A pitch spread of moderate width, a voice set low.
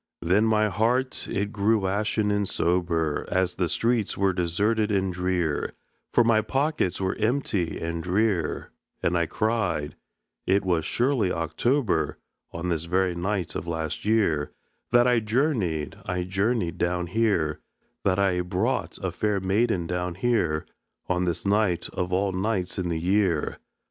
Yes: average, 3.8 semitones; very low, 95 Hz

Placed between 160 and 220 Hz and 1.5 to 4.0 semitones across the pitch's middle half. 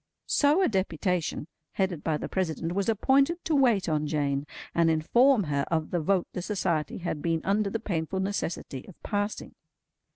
No: medium, 185 Hz; average, 4.7 semitones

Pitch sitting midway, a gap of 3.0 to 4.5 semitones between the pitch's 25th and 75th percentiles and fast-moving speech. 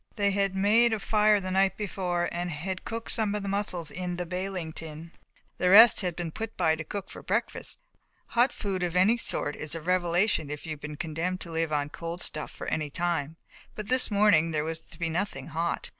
Yes: medium, 180 Hz; average, 3.7 semitones; fast, 225 wpm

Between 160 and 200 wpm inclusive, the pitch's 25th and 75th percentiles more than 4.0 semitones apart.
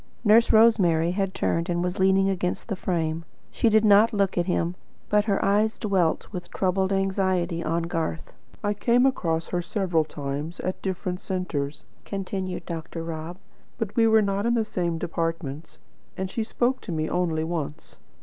No: average, 170 wpm; average, 3.4 semitones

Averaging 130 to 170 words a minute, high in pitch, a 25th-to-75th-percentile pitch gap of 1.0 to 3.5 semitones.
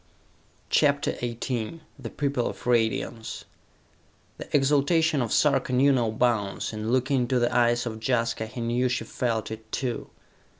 No: average, 145 wpm; low, 120 Hz; average, 2.8 semitones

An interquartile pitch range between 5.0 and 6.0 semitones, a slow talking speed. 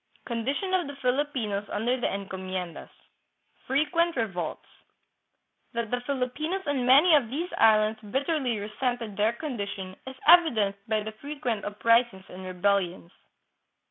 Yes: wide, 5.5 semitones; slow, 125 wpm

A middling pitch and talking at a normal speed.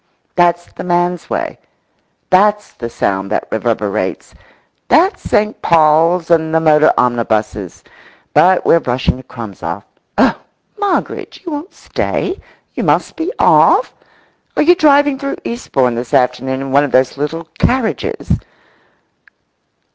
No: medium, 160 Hz; slow, 130 wpm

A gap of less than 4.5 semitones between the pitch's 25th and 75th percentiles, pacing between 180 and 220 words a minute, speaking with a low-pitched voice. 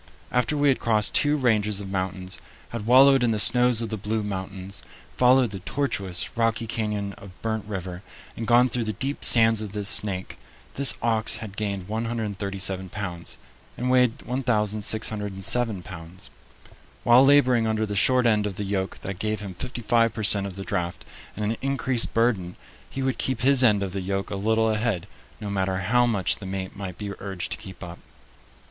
Yes: average, 3.4 semitones; average, 190 wpm; low, 105 Hz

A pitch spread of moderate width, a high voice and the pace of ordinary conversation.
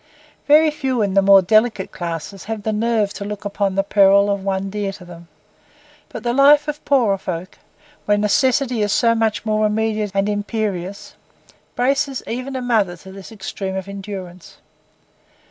Yes: average, 3.0 semitones; high, 205 Hz; average, 170 wpm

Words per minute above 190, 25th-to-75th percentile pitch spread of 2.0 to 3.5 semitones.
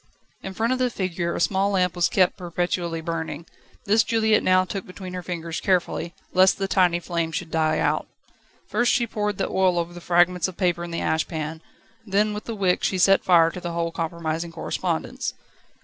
Yes: average, 200 wpm; narrow, 2.5 semitones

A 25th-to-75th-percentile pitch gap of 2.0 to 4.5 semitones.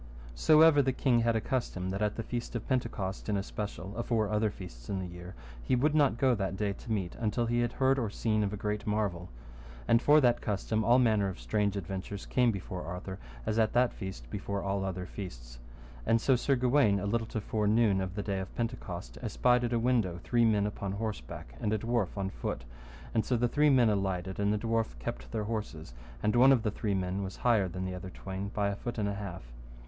Yes: average, 3.7 semitones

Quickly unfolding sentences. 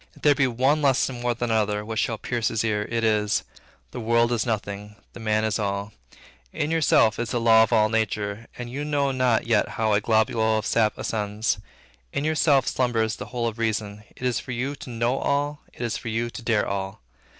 Yes: fast, 215 wpm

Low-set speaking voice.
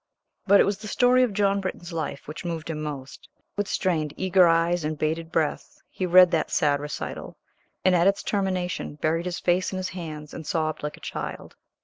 No: medium, 170 Hz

